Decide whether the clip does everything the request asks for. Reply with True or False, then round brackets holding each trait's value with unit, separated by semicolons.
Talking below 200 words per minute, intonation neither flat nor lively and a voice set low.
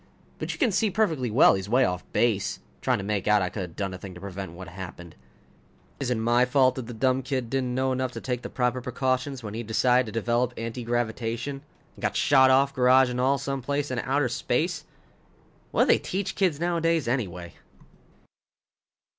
False (205 wpm; 3.3 semitones; 125 Hz)